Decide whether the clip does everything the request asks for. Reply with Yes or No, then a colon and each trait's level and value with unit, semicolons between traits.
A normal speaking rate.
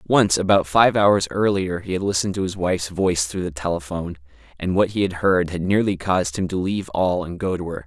No: fast, 235 wpm